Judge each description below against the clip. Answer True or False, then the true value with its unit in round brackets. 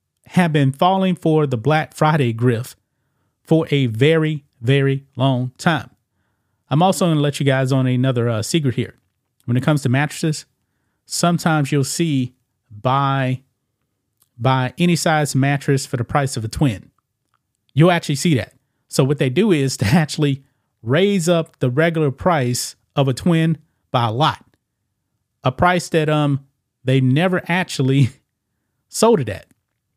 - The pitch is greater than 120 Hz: True (135 Hz)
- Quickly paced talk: False (155 wpm)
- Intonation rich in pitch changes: False (3.9 semitones)